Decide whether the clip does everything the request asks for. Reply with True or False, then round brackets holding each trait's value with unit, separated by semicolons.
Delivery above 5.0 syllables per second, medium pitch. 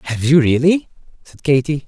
True (5.2 syllables/s; 145 Hz)